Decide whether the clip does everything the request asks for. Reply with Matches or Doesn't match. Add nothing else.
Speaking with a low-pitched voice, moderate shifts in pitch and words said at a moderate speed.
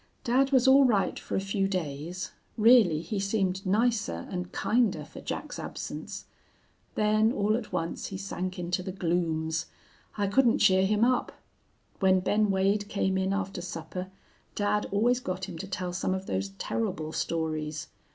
Doesn't match